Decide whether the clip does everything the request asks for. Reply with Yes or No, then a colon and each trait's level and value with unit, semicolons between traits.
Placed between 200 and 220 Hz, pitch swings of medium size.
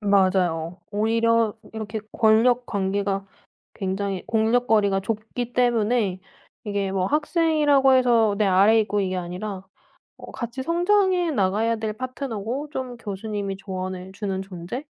Yes: high, 215 Hz; average, 4.0 semitones